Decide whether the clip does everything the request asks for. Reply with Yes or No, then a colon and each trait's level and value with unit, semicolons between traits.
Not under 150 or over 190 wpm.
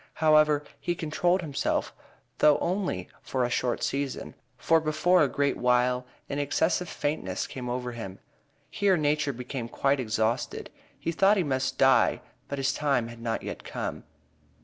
Yes: average, 155 wpm